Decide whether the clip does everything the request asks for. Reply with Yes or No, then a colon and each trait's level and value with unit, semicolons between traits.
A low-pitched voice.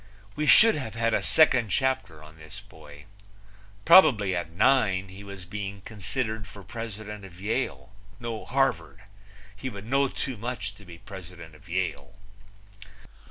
Yes: low, 105 Hz